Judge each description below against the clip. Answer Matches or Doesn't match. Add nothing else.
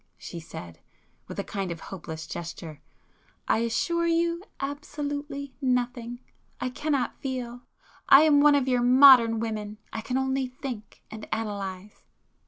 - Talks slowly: Matches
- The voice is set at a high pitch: Matches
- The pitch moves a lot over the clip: Doesn't match